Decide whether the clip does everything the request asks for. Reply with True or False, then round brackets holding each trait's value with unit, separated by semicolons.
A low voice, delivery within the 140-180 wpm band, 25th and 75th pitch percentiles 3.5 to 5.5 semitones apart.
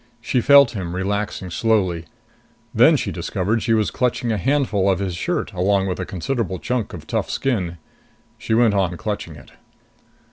True (100 Hz; 170 wpm; 4.1 semitones)